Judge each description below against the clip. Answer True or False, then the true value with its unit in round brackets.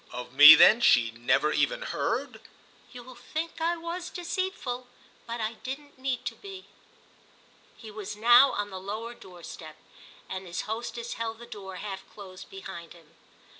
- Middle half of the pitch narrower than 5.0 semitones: False (5.5 semitones)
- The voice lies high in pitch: True (225 Hz)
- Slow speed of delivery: False (160 wpm)